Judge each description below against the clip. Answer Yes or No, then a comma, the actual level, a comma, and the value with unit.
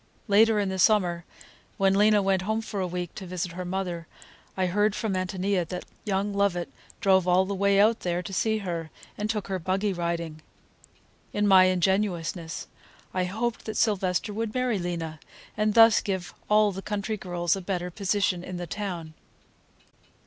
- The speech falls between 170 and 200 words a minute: Yes, average, 175 wpm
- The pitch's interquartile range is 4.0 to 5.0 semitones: No, narrow, 2.6 semitones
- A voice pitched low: No, high, 190 Hz